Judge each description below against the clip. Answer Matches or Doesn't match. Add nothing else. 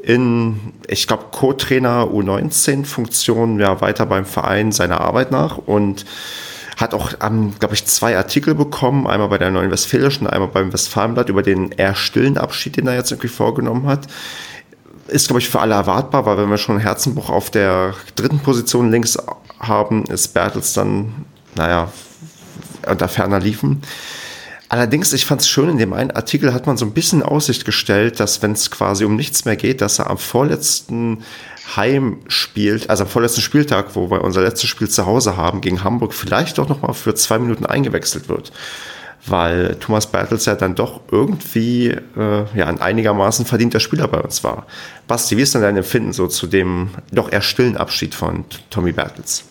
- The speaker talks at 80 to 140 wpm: Doesn't match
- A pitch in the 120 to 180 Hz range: Doesn't match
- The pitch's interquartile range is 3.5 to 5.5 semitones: Matches